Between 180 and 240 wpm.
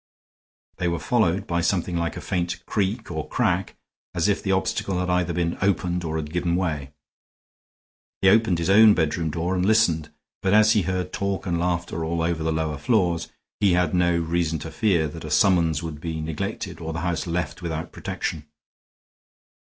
Yes: average, 185 wpm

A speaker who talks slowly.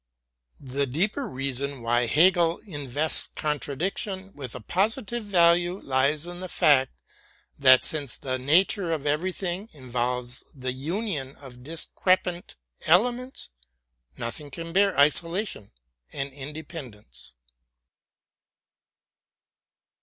Yes: slow, 110 wpm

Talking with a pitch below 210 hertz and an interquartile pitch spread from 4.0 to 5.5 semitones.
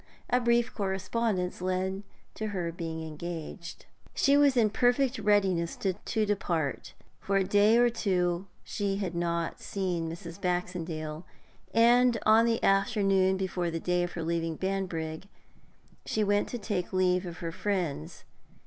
No: high, 190 Hz; average, 3.5 semitones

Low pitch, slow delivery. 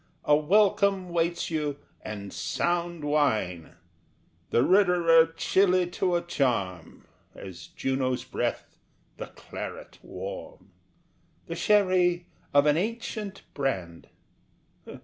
No: medium, 165 Hz; slow, 100 wpm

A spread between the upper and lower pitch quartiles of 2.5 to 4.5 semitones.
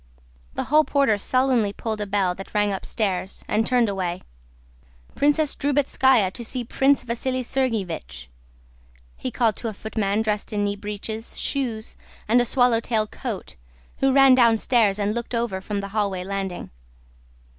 Yes: average, 3.9 semitones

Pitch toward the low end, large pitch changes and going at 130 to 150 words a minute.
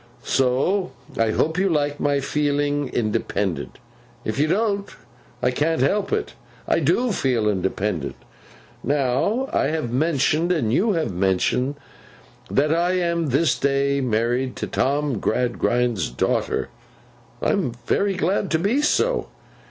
No: medium, 145 Hz; wide, 5.8 semitones; slow, 135 wpm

